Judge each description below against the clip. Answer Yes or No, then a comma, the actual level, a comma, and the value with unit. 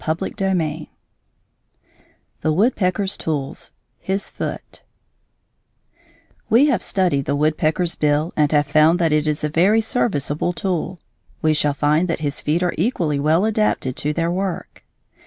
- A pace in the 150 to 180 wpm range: No, average, 140 wpm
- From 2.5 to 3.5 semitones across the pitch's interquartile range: No, average, 4.0 semitones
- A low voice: No, medium, 160 Hz